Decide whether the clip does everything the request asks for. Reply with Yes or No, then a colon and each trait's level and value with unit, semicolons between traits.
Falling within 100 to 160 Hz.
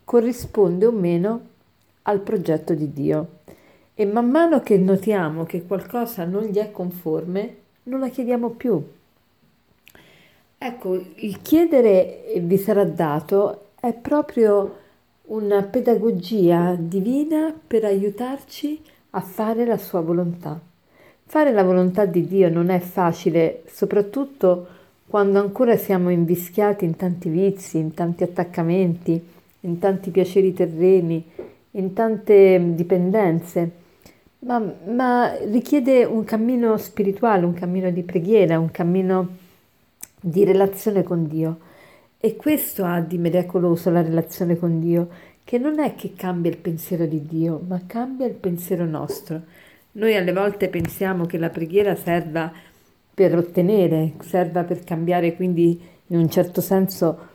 No: high, 190 Hz